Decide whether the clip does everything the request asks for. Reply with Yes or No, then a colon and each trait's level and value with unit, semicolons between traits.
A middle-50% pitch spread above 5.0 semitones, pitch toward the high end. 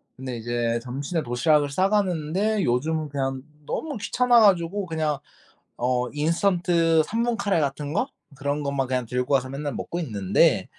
No: wide, 5.5 semitones; medium, 150 Hz